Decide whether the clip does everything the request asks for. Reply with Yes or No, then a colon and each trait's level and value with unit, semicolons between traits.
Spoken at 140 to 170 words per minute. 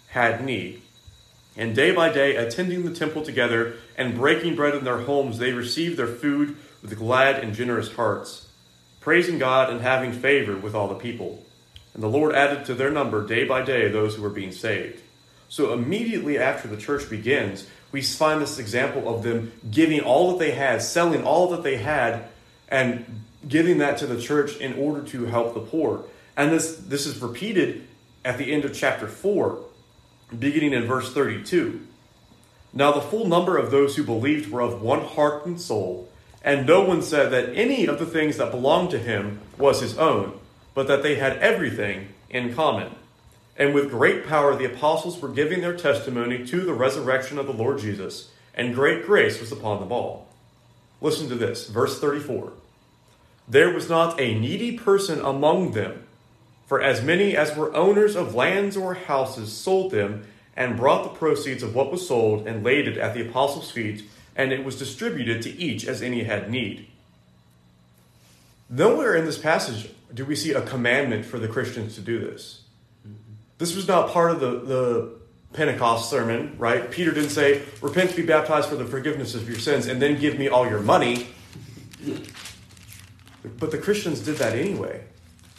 No: average, 180 wpm